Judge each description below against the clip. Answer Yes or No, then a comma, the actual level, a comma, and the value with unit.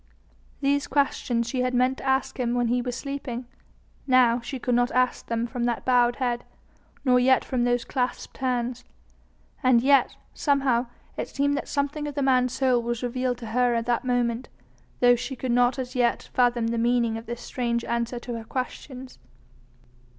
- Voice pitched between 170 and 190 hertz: No, high, 245 Hz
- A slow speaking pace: No, average, 185 wpm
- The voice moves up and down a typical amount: No, narrow, 1.5 semitones